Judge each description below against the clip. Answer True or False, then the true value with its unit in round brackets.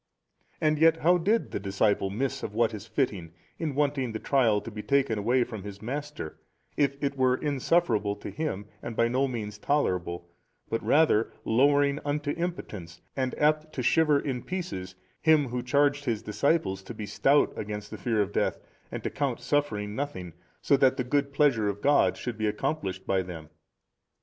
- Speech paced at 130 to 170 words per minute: False (185 wpm)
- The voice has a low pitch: True (125 Hz)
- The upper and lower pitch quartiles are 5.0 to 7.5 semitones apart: True (5.6 semitones)